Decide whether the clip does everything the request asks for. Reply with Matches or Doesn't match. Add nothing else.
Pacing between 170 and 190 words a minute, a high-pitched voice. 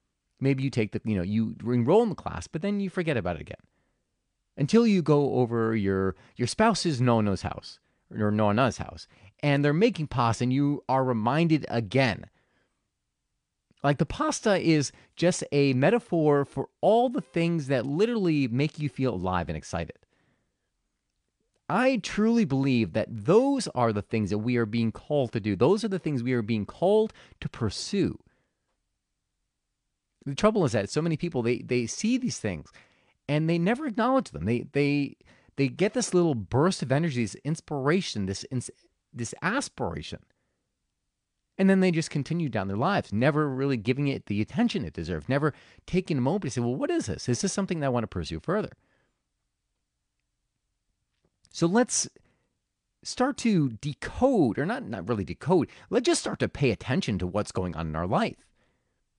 Doesn't match